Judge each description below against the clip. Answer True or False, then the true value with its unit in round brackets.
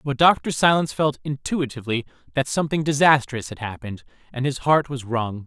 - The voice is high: False (135 Hz)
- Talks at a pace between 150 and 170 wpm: True (165 wpm)